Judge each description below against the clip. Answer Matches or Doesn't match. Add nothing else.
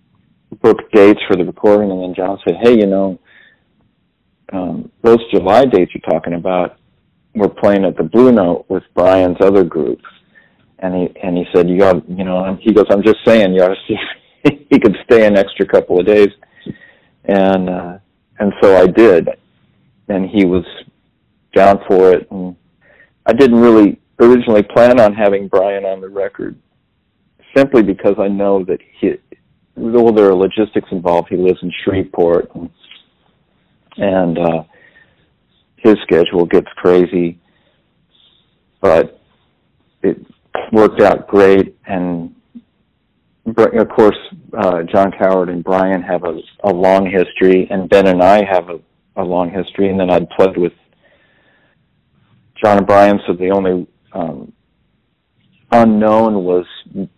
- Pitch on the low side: Matches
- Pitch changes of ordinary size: Doesn't match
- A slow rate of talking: Doesn't match